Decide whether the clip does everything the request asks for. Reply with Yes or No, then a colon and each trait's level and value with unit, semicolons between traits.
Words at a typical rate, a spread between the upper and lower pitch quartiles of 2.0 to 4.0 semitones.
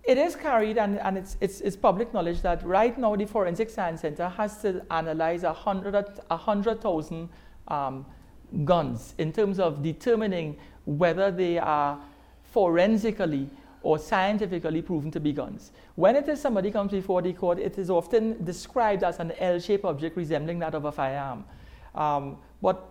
No: average, 160 wpm; average, 4.5 semitones